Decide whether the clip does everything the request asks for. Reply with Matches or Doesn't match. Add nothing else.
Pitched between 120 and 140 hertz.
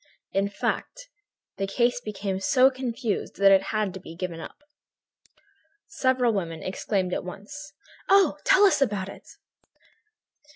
Doesn't match